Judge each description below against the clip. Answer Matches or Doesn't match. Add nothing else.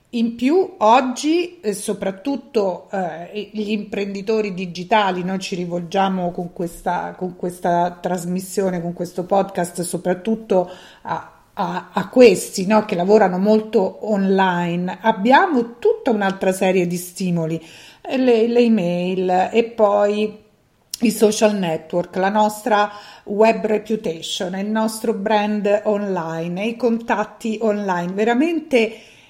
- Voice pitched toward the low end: Doesn't match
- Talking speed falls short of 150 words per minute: Matches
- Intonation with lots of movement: Doesn't match